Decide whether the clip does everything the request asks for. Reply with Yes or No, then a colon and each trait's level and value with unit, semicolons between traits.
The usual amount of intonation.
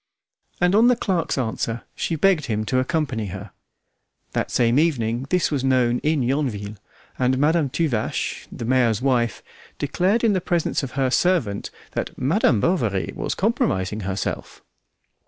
No: wide, 6.5 semitones